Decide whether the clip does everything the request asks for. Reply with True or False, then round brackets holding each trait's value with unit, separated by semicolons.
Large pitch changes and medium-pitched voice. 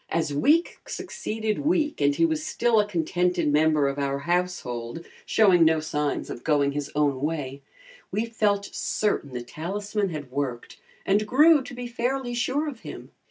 True (7.4 semitones; 170 Hz)